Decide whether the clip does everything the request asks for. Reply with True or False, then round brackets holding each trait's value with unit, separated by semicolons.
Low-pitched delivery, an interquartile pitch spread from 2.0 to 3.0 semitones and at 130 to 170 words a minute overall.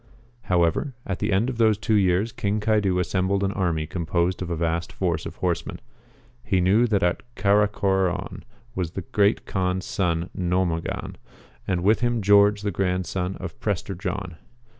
True (95 Hz; 2.6 semitones; 165 wpm)